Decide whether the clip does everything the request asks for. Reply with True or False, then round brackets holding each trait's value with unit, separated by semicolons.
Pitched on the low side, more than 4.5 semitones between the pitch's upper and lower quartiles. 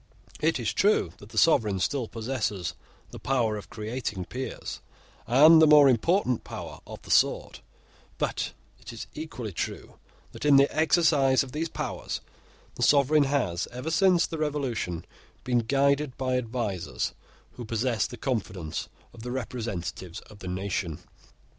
True (125 Hz; 5.0 semitones)